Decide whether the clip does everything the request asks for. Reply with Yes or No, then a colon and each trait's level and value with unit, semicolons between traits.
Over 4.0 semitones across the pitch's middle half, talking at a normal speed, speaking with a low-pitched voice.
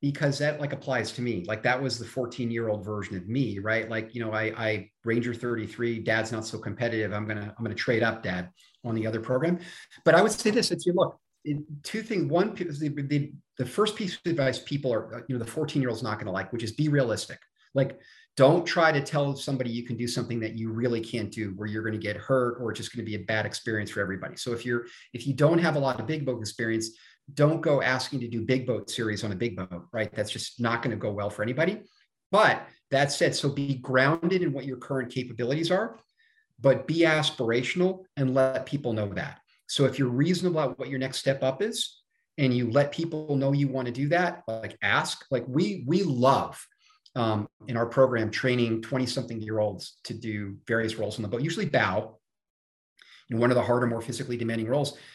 No: average, 4.4 semitones; fast, 230 wpm; low, 125 Hz